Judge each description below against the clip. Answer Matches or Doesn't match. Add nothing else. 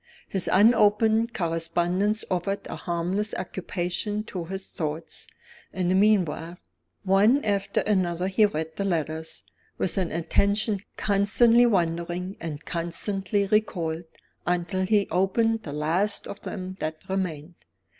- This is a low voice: Doesn't match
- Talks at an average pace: Doesn't match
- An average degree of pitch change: Matches